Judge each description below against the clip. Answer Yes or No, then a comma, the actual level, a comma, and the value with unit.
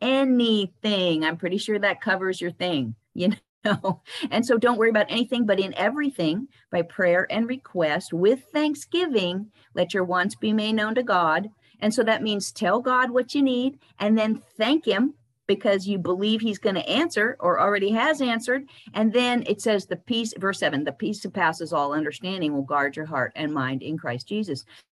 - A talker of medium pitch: No, high, 205 Hz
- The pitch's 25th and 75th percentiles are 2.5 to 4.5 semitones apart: No, average, 5.0 semitones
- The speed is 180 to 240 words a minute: Yes, average, 190 wpm